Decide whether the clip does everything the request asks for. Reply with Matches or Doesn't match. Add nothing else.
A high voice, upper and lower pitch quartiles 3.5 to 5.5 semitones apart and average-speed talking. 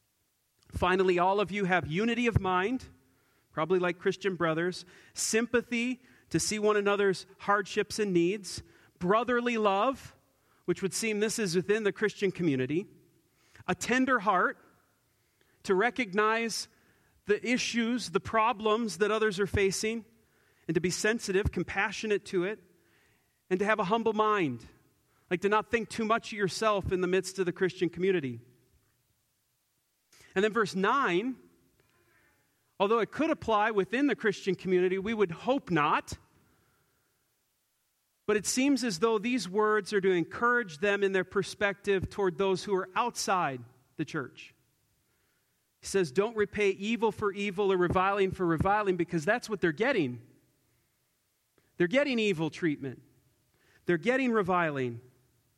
Matches